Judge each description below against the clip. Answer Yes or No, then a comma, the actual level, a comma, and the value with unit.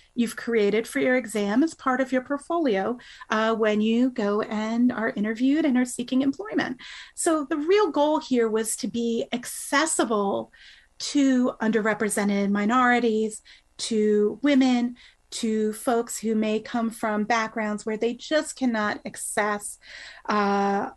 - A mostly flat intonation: No, average, 3.3 semitones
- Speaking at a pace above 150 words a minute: No, slow, 135 wpm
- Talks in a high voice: Yes, high, 230 Hz